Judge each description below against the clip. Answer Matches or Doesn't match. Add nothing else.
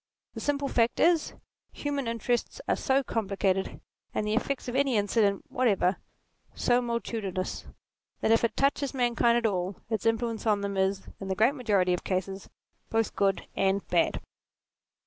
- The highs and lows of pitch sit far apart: Doesn't match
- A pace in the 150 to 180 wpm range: Matches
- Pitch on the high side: Matches